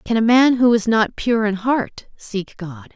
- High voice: Yes, high, 225 Hz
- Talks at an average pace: No, fast, 225 wpm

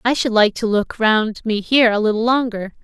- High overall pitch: Yes, high, 225 Hz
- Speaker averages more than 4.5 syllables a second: Yes, 5.3 syllables/s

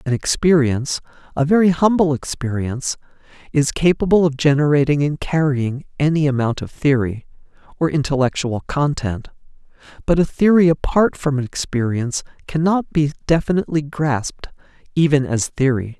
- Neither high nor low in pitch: Yes, medium, 145 Hz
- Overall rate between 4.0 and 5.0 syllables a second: Yes, 4.9 syllables/s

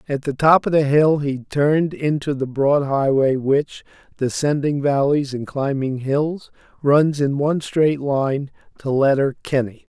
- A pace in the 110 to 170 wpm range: Yes, average, 150 wpm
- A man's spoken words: Yes, male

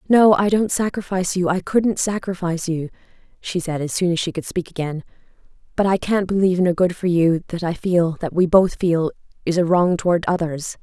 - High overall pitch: No, medium, 180 Hz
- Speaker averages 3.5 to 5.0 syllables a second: No, 5.6 syllables/s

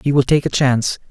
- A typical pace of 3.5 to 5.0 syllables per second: No, 6.7 syllables/s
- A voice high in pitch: No, low, 135 Hz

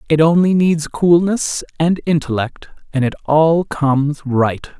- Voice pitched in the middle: Yes, medium, 155 Hz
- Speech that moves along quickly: No, average, 140 wpm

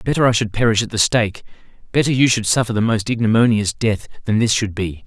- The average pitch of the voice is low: Yes, low, 110 Hz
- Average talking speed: No, fast, 215 wpm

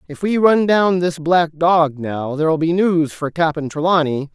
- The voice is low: No, medium, 165 Hz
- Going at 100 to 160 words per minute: No, average, 195 wpm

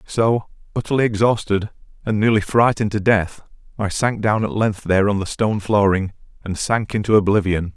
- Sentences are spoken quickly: No, average, 170 wpm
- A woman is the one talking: No, male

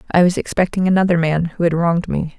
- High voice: No, medium, 170 Hz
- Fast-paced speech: Yes, fast, 225 wpm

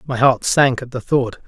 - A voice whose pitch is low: Yes, low, 125 Hz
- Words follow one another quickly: Yes, fast, 245 wpm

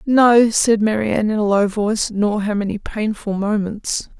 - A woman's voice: Yes, female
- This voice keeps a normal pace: Yes, average, 170 wpm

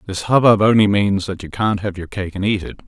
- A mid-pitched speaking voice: No, low, 100 Hz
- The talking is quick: Yes, fast, 270 wpm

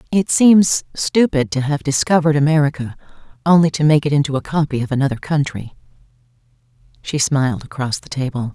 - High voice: No, medium, 140 Hz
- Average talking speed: Yes, average, 155 wpm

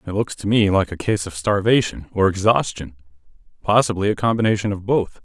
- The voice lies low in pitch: Yes, low, 100 Hz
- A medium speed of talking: Yes, average, 170 wpm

